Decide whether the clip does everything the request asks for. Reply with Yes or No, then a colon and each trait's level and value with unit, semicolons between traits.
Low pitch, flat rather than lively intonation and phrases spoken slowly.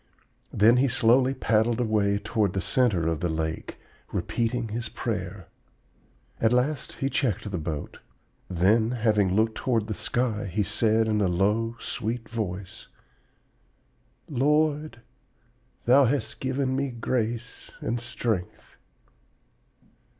No: low, 115 Hz; average, 3.4 semitones; slow, 120 wpm